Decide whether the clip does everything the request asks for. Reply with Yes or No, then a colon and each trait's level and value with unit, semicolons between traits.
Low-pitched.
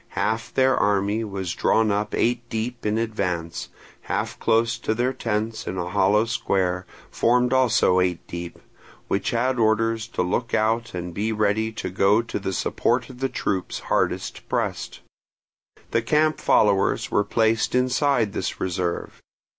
Yes: low, 110 Hz